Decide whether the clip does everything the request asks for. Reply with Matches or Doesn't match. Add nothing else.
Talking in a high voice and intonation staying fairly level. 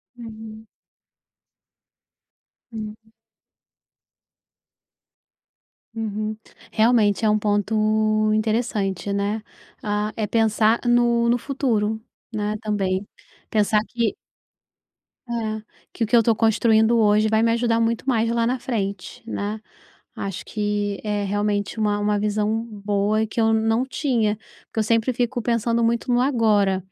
Matches